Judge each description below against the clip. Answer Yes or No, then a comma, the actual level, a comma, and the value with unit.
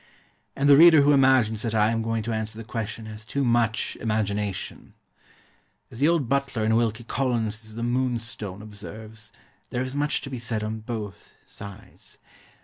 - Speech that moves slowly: No, average, 170 wpm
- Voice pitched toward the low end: Yes, low, 115 Hz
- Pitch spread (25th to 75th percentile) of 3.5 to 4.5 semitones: No, average, 2.9 semitones